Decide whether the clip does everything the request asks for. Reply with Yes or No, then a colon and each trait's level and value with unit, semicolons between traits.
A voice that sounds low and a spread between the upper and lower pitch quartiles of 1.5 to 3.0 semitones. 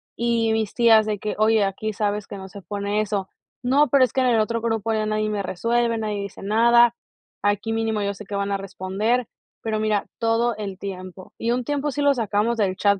No: high, 215 Hz; narrow, 2.4 semitones